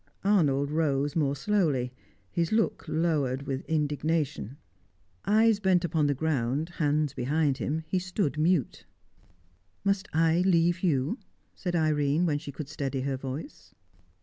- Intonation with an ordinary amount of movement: Yes, average, 3.7 semitones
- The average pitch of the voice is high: No, medium, 155 Hz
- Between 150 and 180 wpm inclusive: No, slow, 135 wpm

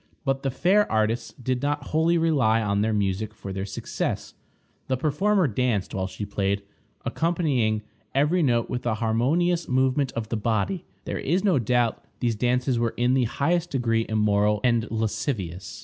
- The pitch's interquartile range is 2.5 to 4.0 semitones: No, average, 4.8 semitones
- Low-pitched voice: Yes, low, 120 Hz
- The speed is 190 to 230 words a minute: No, average, 165 wpm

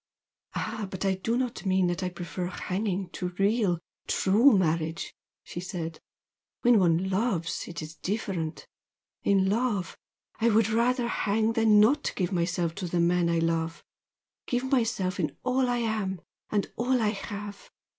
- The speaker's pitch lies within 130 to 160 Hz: No, high, 195 Hz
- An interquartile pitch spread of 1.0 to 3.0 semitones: No, average, 4.2 semitones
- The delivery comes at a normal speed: Yes, average, 155 wpm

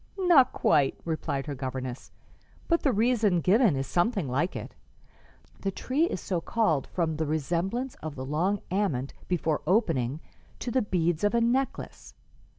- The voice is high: No, medium, 175 Hz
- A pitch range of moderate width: No, wide, 7.4 semitones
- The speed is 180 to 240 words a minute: No, average, 155 wpm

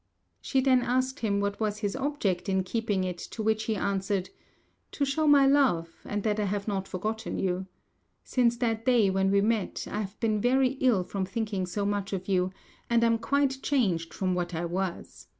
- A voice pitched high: Yes, high, 210 Hz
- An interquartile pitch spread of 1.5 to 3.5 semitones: No, average, 4.0 semitones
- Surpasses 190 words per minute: Yes, average, 200 wpm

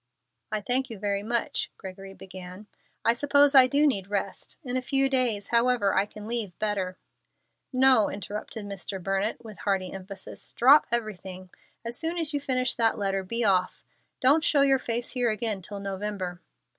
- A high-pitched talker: Yes, high, 215 Hz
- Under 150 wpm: No, average, 175 wpm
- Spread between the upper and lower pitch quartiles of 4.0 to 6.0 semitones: Yes, average, 4.5 semitones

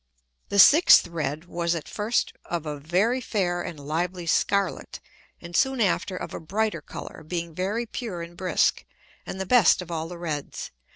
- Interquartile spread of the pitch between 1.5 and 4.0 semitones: Yes, average, 3.4 semitones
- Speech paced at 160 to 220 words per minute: Yes, average, 175 wpm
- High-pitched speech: No, medium, 175 Hz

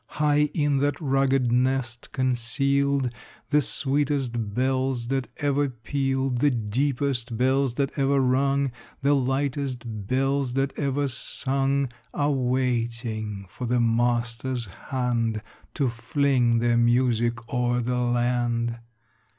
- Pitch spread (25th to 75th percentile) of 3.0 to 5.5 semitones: No, narrow, 2.6 semitones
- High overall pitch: No, low, 130 Hz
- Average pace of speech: No, slow, 115 wpm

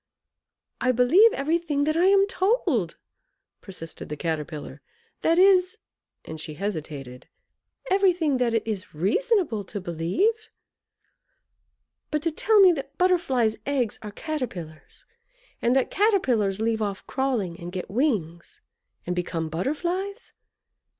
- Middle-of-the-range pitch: No, very high, 250 Hz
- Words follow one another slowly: Yes, slow, 125 wpm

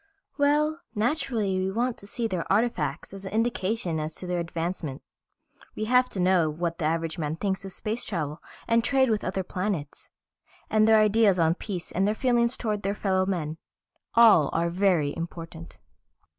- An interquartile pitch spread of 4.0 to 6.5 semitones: Yes, average, 4.9 semitones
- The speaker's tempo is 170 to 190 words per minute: Yes, average, 175 wpm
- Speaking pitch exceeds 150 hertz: Yes, high, 190 Hz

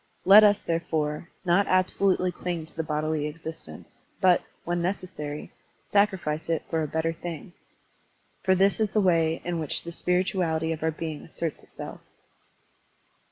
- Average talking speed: Yes, average, 150 wpm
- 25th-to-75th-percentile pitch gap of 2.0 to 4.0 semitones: Yes, narrow, 2.6 semitones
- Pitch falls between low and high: Yes, medium, 165 Hz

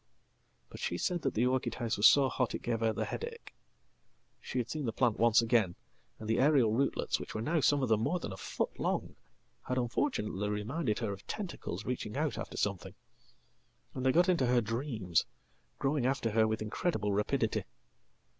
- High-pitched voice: No, low, 120 Hz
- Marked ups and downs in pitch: No, average, 4.2 semitones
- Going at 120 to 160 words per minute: No, average, 180 wpm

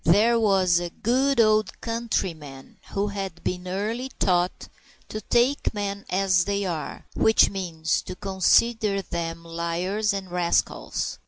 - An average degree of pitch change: Yes, average, 3.6 semitones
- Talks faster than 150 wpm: No, slow, 135 wpm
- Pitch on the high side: Yes, high, 195 Hz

